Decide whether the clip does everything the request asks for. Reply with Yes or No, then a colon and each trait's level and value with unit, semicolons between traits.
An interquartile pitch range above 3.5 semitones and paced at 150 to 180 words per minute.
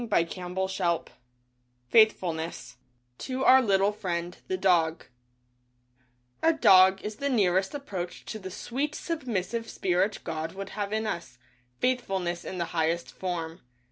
No: average, 4.1 semitones; average, 140 wpm